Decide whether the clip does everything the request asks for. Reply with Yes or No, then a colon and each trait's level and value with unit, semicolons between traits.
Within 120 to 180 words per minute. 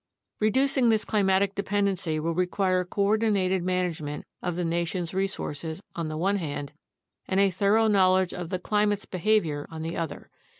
Yes: average, 160 wpm